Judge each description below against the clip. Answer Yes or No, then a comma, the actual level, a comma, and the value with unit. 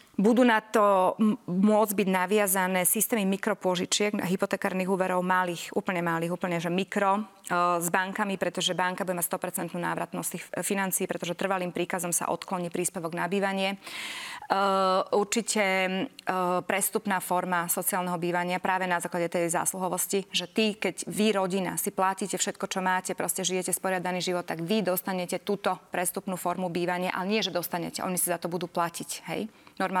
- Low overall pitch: No, medium, 185 Hz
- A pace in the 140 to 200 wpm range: Yes, average, 160 wpm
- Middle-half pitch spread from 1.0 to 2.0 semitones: Yes, narrow, 1.7 semitones